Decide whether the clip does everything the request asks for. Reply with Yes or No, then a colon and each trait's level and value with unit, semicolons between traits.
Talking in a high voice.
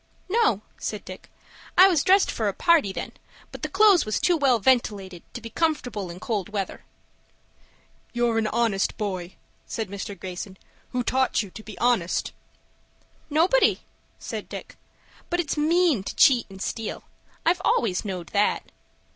Yes: high, 225 Hz